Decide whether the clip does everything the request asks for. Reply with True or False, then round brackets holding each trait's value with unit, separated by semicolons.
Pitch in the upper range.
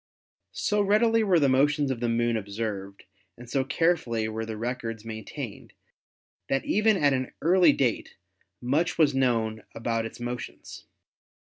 False (125 Hz)